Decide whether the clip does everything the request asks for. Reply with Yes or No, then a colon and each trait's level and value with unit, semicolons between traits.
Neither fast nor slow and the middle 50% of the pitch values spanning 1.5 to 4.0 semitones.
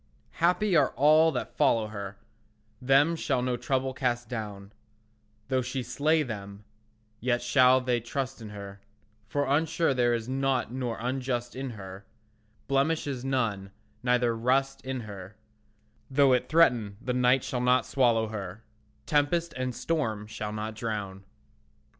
Yes: average, 145 wpm; average, 3.6 semitones